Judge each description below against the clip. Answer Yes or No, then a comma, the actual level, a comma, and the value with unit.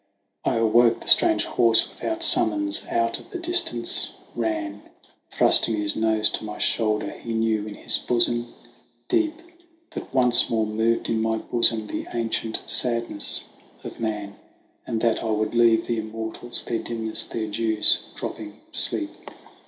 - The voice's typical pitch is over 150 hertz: No, low, 115 Hz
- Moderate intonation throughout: No, narrow, 1.4 semitones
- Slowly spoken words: No, average, 150 wpm